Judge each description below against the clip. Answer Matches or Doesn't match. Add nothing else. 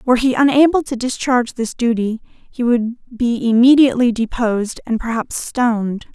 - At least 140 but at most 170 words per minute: Matches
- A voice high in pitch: Matches